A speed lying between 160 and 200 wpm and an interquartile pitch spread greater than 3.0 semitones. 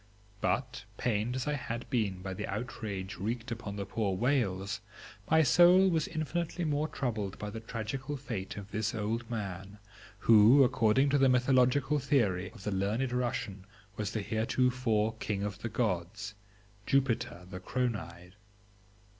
No: average, 150 wpm; average, 4.2 semitones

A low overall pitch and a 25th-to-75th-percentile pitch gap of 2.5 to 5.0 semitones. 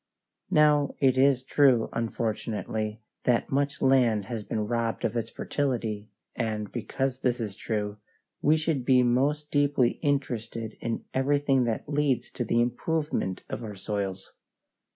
Yes: low, 120 Hz; average, 4.0 semitones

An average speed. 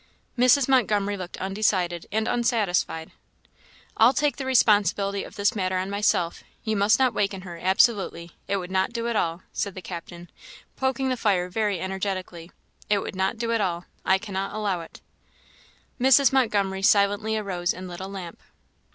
Yes: average, 170 wpm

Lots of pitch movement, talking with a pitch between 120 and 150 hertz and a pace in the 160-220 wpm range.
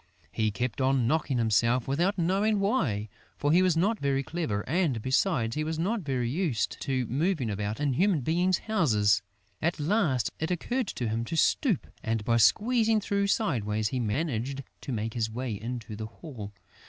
Yes: wide, 7.7 semitones; low, 135 Hz; average, 180 wpm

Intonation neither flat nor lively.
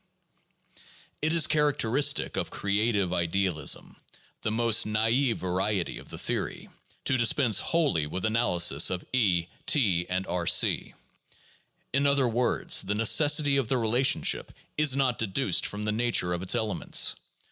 No: wide, 6.0 semitones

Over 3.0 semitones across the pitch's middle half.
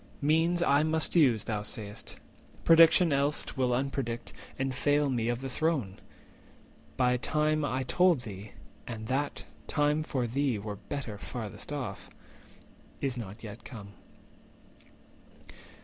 Yes: average, 4.6 semitones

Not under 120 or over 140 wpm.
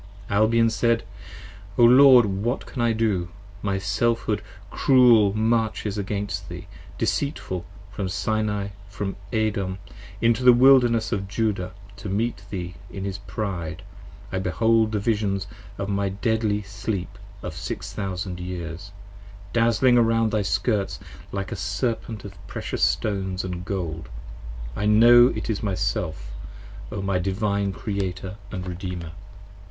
Yes: slow, 135 wpm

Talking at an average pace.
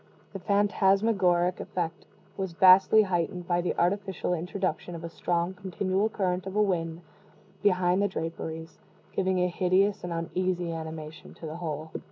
Yes: average, 145 wpm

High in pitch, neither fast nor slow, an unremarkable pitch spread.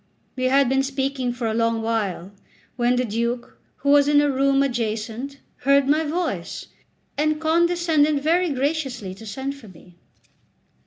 Yes: very high, 270 Hz; average, 155 wpm; average, 4.0 semitones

